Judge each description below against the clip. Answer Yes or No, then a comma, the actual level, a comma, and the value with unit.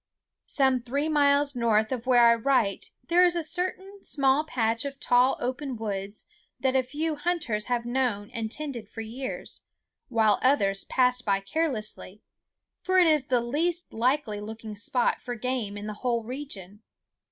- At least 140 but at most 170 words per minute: Yes, average, 165 wpm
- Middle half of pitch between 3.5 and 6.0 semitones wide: Yes, average, 4.5 semitones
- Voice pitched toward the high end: Yes, very high, 250 Hz